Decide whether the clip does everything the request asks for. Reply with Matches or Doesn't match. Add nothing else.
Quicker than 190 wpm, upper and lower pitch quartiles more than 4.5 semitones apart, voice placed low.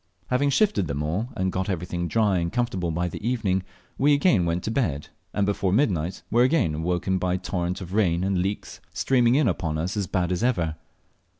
Matches